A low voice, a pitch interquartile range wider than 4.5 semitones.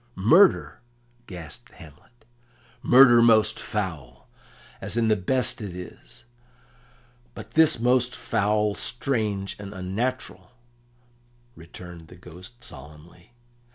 Yes: low, 105 Hz; average, 5.1 semitones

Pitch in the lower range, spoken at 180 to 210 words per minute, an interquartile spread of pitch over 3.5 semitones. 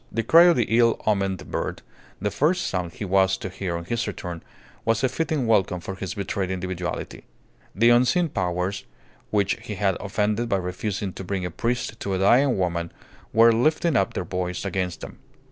Yes: low, 100 Hz; average, 190 wpm; average, 4.2 semitones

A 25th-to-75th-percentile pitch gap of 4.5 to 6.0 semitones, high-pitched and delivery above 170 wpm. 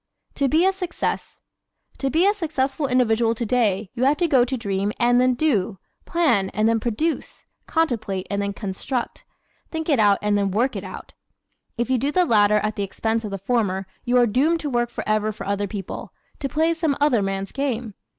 Yes: wide, 5.4 semitones; high, 240 Hz; average, 200 wpm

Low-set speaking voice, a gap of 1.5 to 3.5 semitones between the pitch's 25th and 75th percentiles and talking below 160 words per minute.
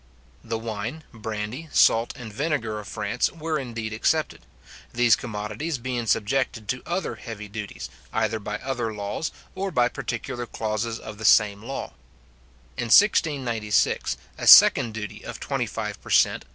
Yes: low, 115 Hz; average, 3.1 semitones; average, 150 wpm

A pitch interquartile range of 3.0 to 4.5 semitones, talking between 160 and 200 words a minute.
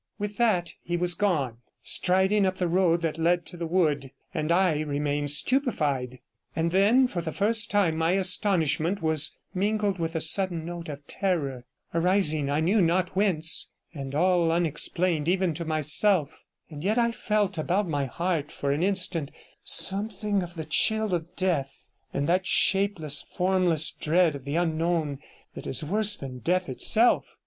Yes: average, 3.7 semitones; average, 165 wpm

